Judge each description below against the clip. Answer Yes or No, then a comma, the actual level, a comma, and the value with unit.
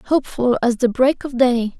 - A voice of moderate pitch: No, very high, 250 Hz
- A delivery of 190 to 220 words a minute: Yes, average, 200 wpm